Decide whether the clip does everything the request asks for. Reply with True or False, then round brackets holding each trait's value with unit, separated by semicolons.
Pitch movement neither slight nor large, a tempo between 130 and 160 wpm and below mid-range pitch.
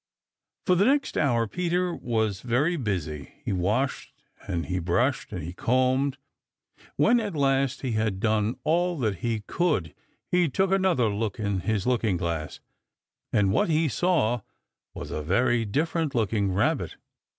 False (7.6 semitones; 150 wpm; 120 Hz)